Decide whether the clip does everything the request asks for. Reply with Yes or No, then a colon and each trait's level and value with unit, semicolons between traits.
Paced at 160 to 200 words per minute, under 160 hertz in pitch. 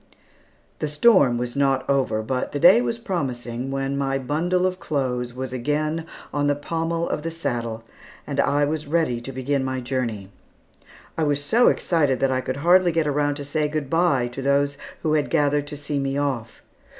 Yes: average, 185 wpm; medium, 140 Hz